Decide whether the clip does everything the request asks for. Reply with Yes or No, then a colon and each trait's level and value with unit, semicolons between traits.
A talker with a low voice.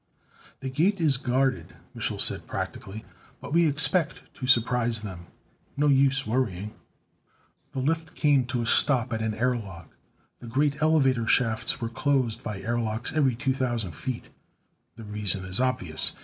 Yes: low, 125 Hz